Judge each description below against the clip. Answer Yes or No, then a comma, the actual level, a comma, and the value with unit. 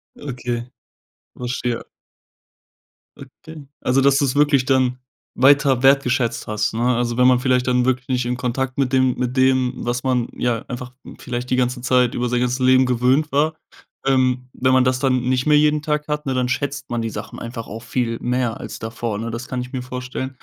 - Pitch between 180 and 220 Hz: No, low, 125 Hz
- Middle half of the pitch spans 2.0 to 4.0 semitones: No, narrow, 1.3 semitones